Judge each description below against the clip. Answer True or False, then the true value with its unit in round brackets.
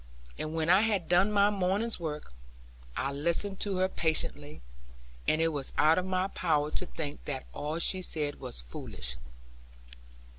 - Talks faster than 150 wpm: True (160 wpm)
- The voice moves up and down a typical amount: True (4.1 semitones)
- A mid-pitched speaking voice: True (165 Hz)